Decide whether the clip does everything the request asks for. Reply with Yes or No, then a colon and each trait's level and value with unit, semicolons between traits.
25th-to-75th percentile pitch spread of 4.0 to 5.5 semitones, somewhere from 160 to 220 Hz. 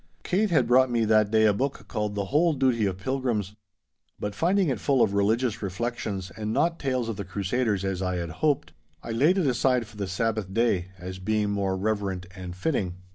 No: average, 4.6 semitones; low, 110 Hz